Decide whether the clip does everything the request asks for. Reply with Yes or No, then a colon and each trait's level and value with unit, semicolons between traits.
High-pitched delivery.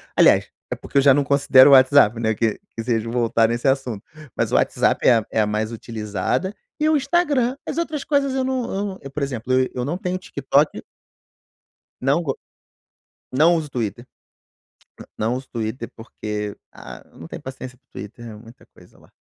No: low, 130 Hz